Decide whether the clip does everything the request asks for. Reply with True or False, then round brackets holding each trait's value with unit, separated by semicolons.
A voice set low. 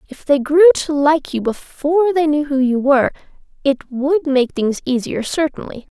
False (290 Hz)